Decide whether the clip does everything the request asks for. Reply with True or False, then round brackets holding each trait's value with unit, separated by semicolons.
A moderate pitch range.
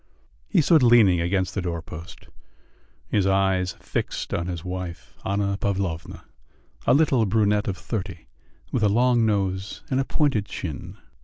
True (3.4 semitones)